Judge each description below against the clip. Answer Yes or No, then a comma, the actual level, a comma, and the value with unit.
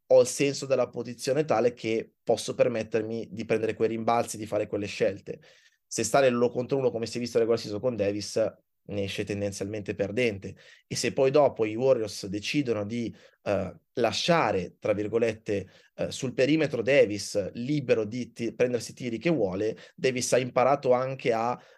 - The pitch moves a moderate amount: Yes, average, 3.3 semitones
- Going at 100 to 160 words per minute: No, fast, 170 wpm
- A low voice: Yes, low, 115 Hz